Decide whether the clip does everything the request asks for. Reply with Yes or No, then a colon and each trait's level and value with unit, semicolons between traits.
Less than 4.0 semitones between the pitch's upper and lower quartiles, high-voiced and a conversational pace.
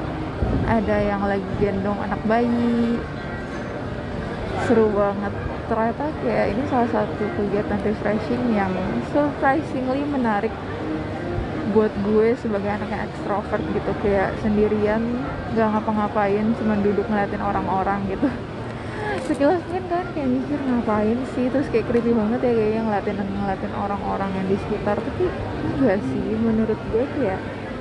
Yes: narrow, 2.5 semitones; high, 220 Hz; average, 125 wpm